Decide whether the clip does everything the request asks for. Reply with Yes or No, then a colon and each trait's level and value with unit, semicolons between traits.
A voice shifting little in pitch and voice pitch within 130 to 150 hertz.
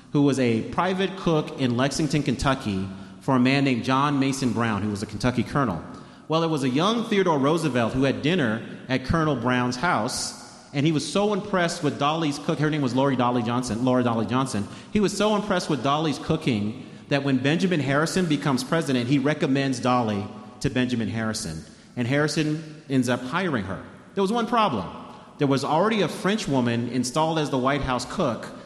No: average, 4.2 semitones; medium, 140 Hz